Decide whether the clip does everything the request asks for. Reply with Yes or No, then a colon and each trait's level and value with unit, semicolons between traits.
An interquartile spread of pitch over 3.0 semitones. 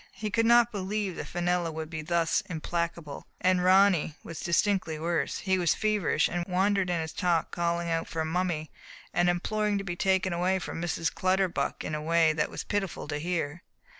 No: narrow, 2.5 semitones